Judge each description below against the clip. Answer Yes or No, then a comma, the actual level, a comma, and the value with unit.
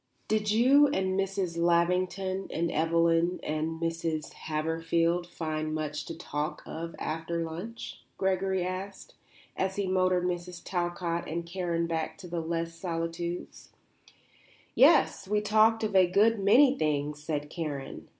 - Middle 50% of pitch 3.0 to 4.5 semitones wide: No, narrow, 2.5 semitones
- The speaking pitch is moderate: Yes, medium, 170 Hz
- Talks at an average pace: No, slow, 130 wpm